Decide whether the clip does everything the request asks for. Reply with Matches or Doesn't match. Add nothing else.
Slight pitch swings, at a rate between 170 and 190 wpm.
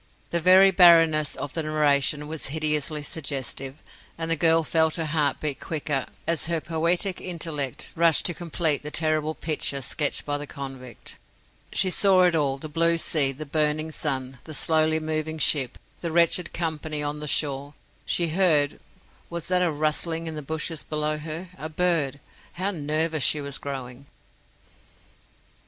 Doesn't match